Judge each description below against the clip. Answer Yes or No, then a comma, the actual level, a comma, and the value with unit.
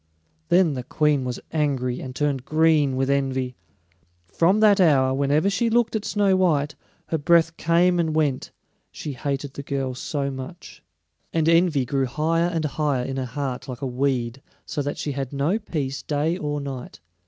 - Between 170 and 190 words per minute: Yes, average, 175 wpm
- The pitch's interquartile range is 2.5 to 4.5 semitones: Yes, average, 3.8 semitones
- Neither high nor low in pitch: Yes, medium, 145 Hz